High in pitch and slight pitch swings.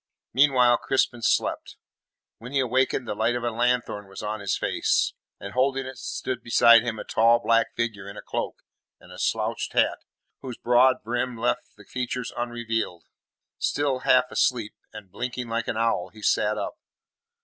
No: low, 120 Hz; narrow, 2.3 semitones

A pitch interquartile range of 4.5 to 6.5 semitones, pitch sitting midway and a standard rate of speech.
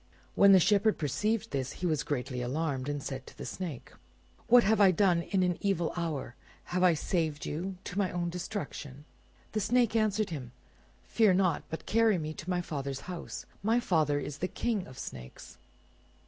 Yes: wide, 5.4 semitones; medium, 175 Hz; average, 190 wpm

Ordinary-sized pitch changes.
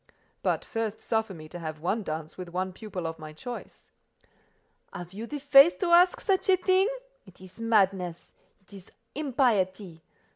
No: wide, 6.5 semitones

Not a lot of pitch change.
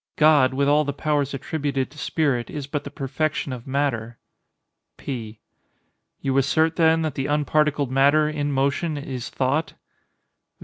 Yes: narrow, 2.3 semitones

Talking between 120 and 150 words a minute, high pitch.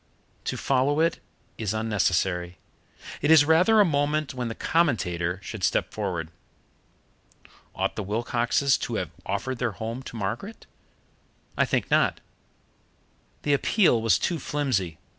No: slow, 135 wpm; low, 120 Hz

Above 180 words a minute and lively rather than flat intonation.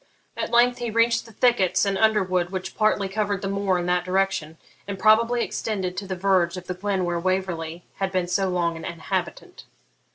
No: average, 195 wpm; average, 2.7 semitones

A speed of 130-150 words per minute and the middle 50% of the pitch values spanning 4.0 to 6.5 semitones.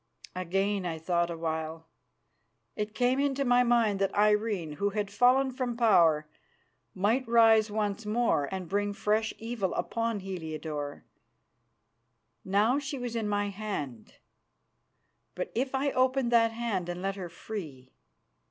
Yes: average, 140 wpm; average, 4.7 semitones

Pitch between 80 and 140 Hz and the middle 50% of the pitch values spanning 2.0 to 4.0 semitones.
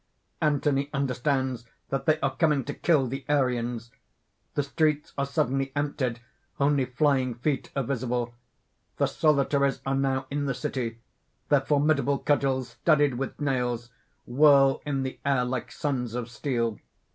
Yes: low, 135 Hz; narrow, 2.4 semitones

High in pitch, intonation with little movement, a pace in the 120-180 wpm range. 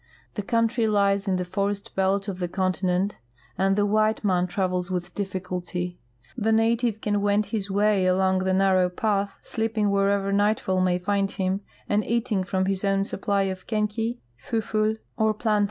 Yes: high, 200 Hz; narrow, 2.2 semitones; average, 170 wpm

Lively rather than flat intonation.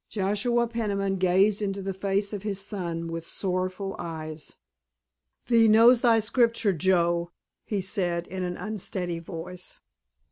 No: average, 3.1 semitones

